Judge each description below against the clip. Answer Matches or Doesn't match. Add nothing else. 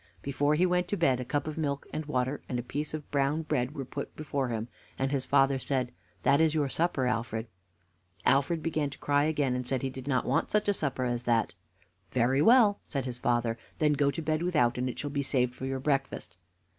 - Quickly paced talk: Matches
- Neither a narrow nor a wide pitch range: Matches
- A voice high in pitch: Doesn't match